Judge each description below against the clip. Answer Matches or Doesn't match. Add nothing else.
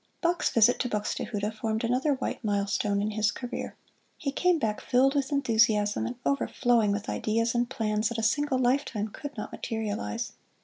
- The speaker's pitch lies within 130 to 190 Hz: Doesn't match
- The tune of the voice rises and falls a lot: Doesn't match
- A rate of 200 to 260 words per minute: Doesn't match